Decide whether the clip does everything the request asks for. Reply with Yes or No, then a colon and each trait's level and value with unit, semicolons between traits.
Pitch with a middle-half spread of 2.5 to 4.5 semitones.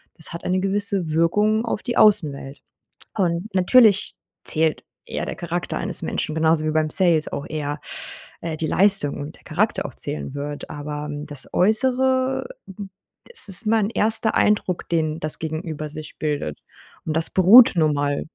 No: average, 5.0 semitones